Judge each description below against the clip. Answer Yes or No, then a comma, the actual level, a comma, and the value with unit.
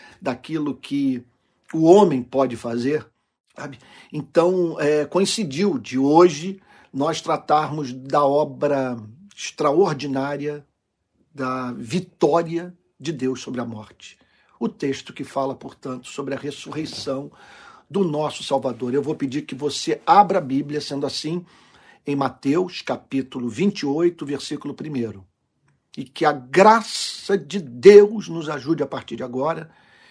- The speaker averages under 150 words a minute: Yes, average, 125 wpm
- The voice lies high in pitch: No, medium, 145 Hz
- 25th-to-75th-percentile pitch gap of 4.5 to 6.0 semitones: No, average, 4.0 semitones